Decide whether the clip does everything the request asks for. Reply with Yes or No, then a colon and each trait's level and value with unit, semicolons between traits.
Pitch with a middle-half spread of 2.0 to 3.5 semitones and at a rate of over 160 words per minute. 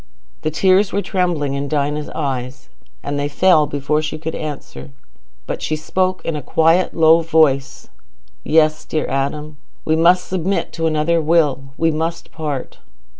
No: narrow, 2.5 semitones; average, 155 wpm